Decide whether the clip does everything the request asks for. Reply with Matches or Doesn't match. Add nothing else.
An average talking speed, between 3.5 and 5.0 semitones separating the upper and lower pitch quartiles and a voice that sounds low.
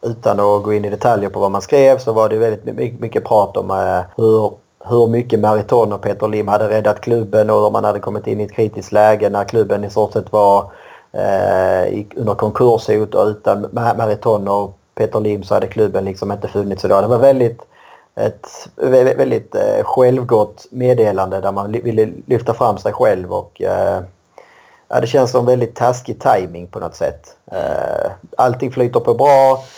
Doesn't match